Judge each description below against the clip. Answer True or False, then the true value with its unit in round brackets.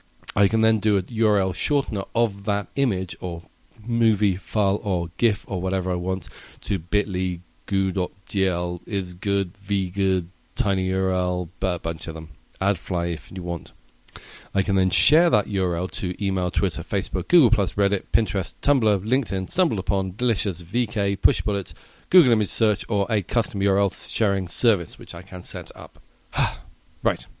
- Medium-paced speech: True (150 wpm)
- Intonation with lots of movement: False (2.6 semitones)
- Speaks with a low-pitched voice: True (95 Hz)